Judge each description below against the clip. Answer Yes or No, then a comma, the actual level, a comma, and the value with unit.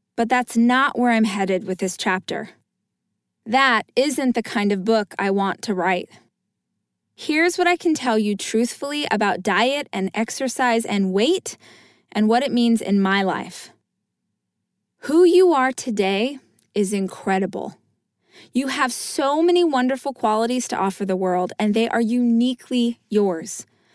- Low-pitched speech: No, high, 230 Hz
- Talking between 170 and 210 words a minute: No, average, 150 wpm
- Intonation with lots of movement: No, average, 4.8 semitones